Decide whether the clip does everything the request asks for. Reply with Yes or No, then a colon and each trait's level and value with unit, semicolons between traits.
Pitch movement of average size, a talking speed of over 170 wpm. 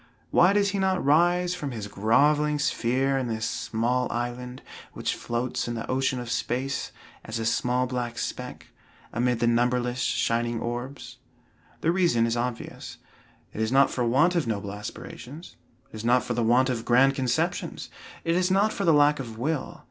Yes: average, 3.8 semitones; average, 180 wpm